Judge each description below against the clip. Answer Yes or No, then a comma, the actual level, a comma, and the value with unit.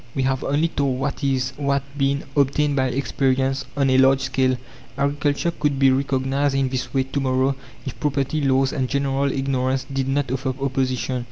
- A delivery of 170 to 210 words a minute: Yes, average, 180 wpm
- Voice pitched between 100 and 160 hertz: Yes, low, 135 Hz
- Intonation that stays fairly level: Yes, narrow, 1.1 semitones